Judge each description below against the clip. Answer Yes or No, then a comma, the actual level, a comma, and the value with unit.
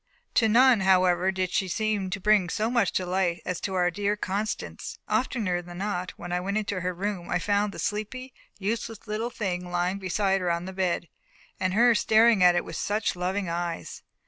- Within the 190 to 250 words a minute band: Yes, average, 200 wpm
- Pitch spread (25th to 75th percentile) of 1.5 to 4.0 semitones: Yes, average, 2.9 semitones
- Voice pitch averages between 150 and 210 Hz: Yes, high, 190 Hz